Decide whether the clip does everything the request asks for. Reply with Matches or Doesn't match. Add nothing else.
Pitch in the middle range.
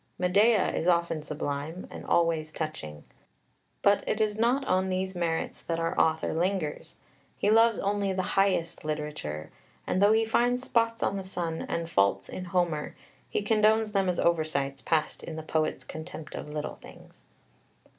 Matches